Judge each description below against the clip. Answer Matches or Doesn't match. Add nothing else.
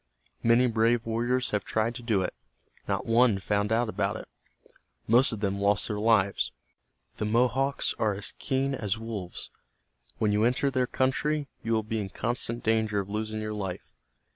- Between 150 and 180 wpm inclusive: Matches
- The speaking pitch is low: Matches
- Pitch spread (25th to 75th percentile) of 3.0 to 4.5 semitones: Doesn't match